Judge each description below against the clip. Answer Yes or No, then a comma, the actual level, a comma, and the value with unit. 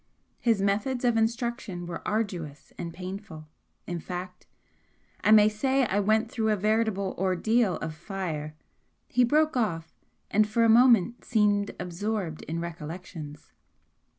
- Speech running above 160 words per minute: No, average, 140 wpm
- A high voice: Yes, high, 205 Hz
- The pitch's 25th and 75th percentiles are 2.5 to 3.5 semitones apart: No, average, 4.4 semitones